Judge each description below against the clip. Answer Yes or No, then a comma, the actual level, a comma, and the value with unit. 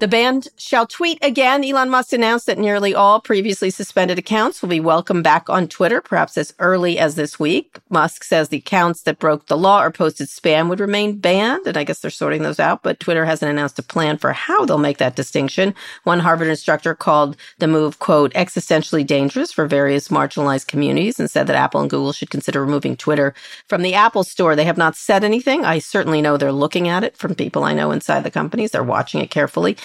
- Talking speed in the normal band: No, fast, 220 wpm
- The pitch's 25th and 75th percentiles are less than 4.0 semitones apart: No, wide, 5.4 semitones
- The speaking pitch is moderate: Yes, medium, 165 Hz